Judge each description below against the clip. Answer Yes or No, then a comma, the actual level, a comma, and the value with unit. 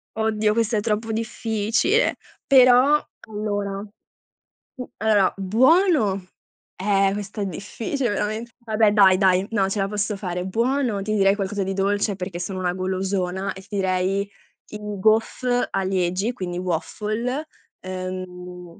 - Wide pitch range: No, average, 2.8 semitones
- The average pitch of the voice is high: Yes, high, 205 Hz